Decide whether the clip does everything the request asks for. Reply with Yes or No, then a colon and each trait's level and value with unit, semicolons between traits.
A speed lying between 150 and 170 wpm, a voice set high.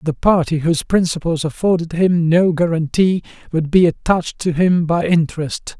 No: average, 155 wpm; medium, 165 Hz